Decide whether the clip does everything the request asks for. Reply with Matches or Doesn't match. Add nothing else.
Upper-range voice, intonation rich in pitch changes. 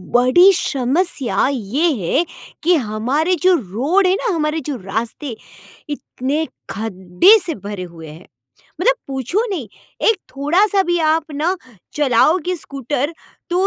Matches